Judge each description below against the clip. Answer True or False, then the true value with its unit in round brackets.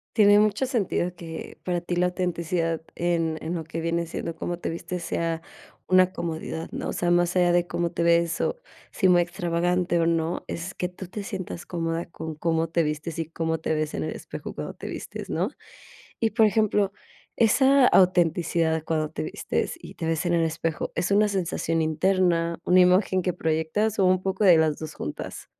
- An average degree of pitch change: False (2.0 semitones)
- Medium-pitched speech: True (170 Hz)